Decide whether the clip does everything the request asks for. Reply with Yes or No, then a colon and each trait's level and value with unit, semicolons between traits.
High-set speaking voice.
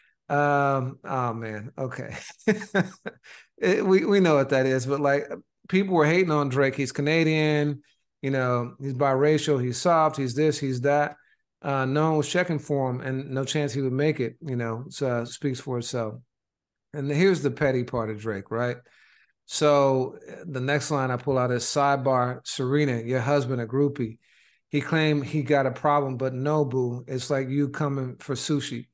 No: medium, 140 Hz